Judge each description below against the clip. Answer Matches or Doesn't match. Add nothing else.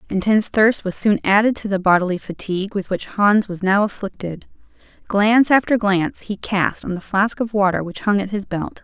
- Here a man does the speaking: Doesn't match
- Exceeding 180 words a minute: Matches